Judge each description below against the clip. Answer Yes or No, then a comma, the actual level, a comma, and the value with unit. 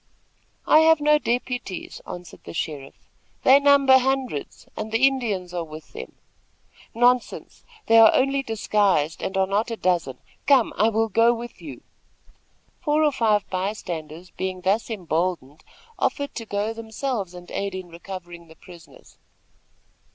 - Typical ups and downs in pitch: No, wide, 5.8 semitones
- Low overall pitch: No, high, 210 Hz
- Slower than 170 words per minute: Yes, average, 150 wpm